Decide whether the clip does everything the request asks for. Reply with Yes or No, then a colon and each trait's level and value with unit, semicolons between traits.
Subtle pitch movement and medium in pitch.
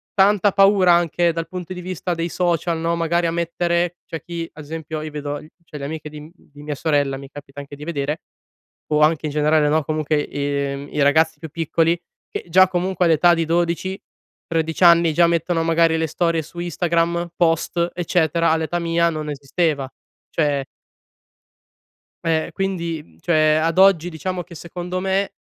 Yes: narrow, 2.3 semitones; medium, 165 Hz